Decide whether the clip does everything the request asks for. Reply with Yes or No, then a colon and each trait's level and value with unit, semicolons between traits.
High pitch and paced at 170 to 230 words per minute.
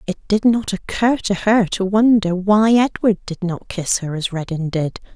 Yes: high, 195 Hz; average, 200 wpm